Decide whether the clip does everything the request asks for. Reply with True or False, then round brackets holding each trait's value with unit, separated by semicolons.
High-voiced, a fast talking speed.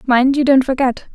True (265 Hz; 210 wpm)